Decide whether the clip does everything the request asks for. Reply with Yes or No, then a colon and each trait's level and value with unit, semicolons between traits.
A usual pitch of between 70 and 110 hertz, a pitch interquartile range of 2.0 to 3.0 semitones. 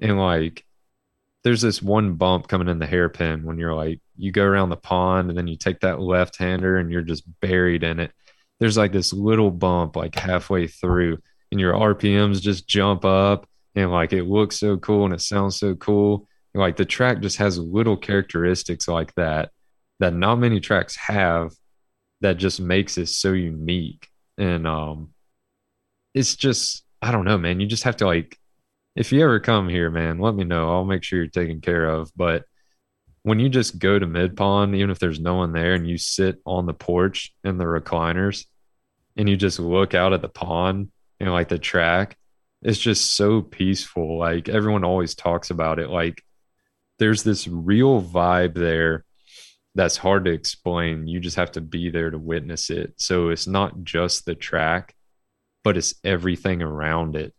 Yes: very low, 90 Hz; average, 2.7 semitones